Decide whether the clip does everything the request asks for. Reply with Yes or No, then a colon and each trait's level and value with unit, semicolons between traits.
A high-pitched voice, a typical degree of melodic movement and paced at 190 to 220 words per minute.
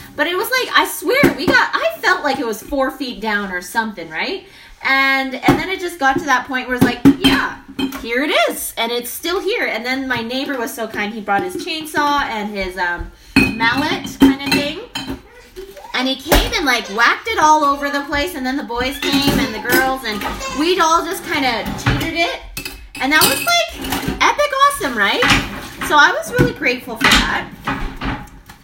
Yes: very high, 275 Hz; average, 4.5 semitones; fast, 205 wpm